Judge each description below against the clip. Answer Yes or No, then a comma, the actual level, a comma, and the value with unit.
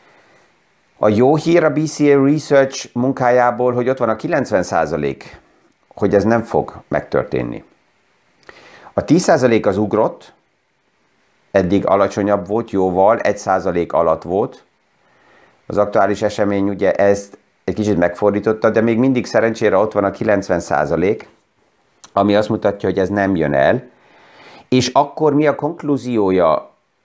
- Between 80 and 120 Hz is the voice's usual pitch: Yes, low, 110 Hz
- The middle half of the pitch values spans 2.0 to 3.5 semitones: No, average, 4.3 semitones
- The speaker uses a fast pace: No, average, 125 wpm